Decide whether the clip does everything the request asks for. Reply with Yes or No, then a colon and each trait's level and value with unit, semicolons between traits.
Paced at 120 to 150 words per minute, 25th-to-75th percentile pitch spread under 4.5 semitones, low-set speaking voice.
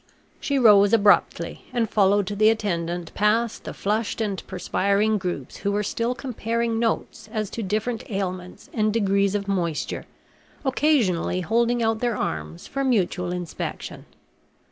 No: average, 140 wpm; average, 3.4 semitones; high, 210 Hz